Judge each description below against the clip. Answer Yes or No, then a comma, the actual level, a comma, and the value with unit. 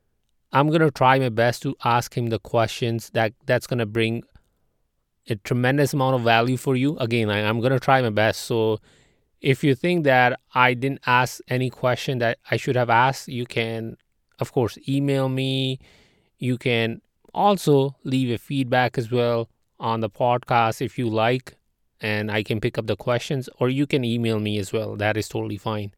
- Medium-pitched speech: No, low, 125 Hz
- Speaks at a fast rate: No, average, 195 wpm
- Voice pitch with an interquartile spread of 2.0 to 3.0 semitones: Yes, average, 2.7 semitones